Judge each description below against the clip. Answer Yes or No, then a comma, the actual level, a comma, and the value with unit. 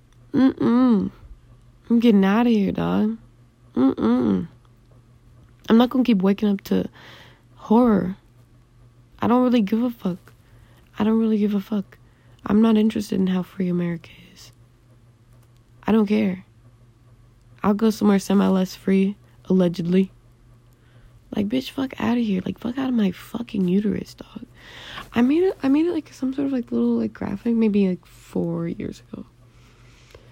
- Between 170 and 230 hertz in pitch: Yes, high, 190 Hz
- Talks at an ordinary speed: Yes, average, 155 wpm